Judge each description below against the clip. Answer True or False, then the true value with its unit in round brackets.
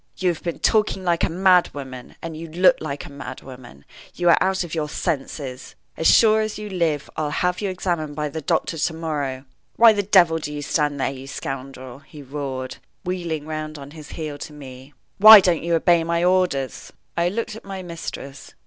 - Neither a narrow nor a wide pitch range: True (4.2 semitones)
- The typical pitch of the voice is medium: True (160 Hz)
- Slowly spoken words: False (205 wpm)